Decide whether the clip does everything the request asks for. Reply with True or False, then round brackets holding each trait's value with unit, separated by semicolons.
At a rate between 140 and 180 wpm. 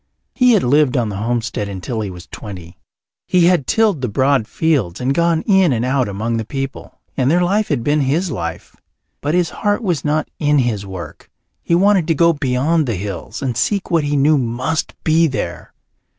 False (200 wpm)